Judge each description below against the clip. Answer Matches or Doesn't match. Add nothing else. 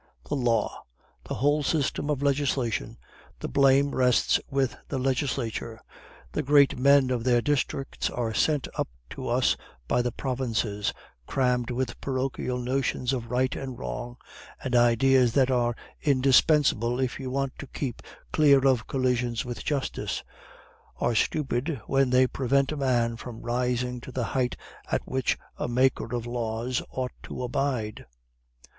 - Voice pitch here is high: Doesn't match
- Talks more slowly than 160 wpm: Matches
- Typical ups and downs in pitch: Doesn't match